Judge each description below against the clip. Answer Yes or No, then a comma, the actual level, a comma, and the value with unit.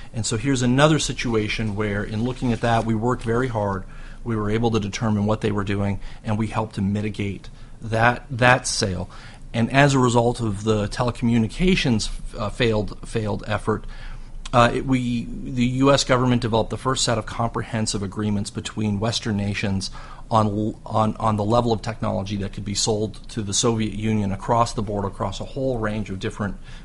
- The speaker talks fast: No, average, 185 wpm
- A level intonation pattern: Yes, narrow, 2.3 semitones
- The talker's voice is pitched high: No, low, 110 Hz